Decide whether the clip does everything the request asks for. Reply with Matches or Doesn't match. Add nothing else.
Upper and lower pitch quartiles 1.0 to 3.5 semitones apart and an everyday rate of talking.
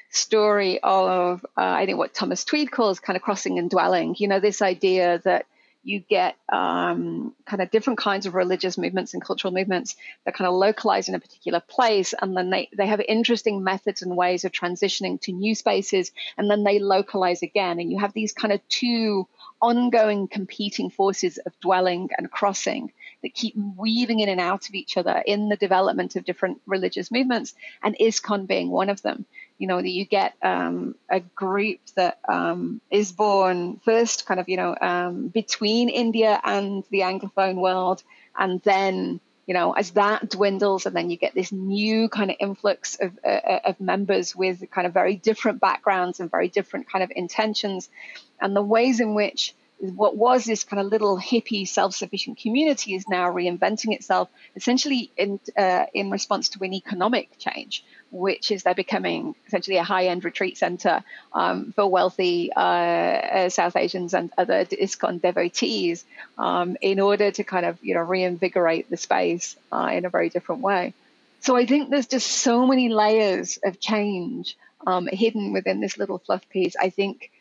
Matches